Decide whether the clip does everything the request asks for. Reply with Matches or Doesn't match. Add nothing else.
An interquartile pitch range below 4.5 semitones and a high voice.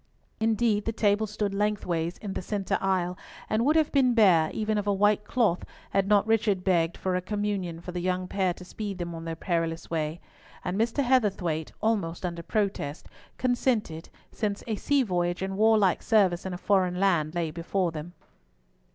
Matches